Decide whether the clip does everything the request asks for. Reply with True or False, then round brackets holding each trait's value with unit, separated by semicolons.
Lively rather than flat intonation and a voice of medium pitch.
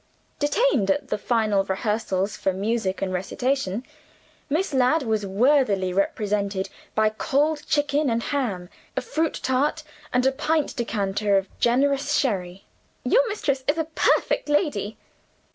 False (6.5 semitones; 235 Hz)